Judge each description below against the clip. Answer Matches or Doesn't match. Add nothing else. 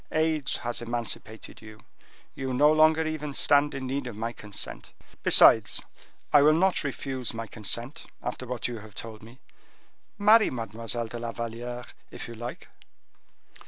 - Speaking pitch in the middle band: Doesn't match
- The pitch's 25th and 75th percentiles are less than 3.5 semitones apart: Doesn't match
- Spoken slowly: Doesn't match